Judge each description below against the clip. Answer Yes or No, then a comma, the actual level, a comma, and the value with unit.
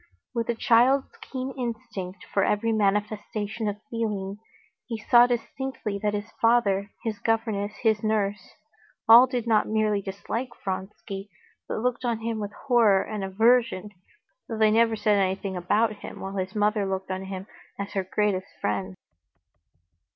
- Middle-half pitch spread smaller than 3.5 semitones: Yes, narrow, 2.6 semitones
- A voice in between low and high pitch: No, high, 210 Hz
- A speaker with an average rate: Yes, average, 150 wpm